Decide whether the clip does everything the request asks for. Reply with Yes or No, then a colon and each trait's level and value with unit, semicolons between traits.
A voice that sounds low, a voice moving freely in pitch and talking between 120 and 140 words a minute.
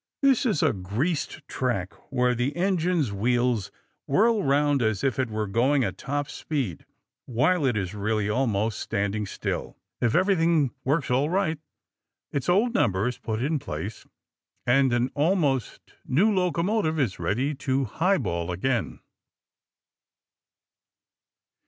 Yes: low, 130 Hz; wide, 6.6 semitones; slow, 135 wpm